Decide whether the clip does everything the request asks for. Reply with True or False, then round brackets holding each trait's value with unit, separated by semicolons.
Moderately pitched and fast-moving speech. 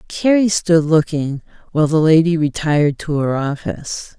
False (160 Hz; 145 wpm)